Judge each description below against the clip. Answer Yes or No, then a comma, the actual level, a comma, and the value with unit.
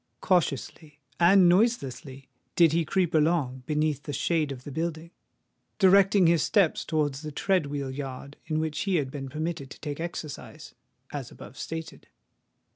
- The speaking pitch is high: No, medium, 155 Hz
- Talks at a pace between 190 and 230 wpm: No, average, 150 wpm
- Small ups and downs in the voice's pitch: No, average, 3.2 semitones